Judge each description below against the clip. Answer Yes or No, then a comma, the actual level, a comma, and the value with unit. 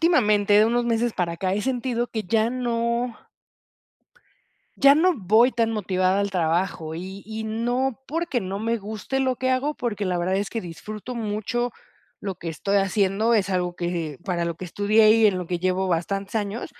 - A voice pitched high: Yes, high, 210 Hz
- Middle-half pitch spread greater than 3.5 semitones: Yes, average, 4.2 semitones